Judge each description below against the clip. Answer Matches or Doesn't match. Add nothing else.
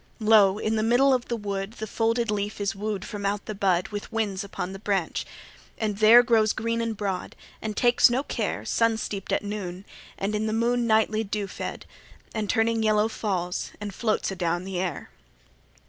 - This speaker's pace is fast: Doesn't match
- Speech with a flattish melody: Matches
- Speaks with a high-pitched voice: Matches